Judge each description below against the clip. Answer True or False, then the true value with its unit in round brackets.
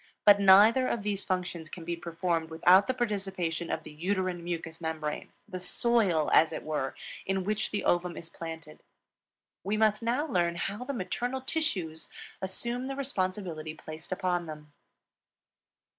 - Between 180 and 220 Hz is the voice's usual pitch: True (185 Hz)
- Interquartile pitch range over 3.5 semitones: True (4.3 semitones)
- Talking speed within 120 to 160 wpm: True (155 wpm)